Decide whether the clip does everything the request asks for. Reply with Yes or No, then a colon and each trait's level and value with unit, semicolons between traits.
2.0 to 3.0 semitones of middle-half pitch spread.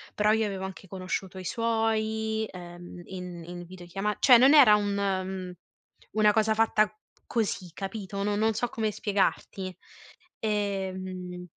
Yes: average, 2.7 semitones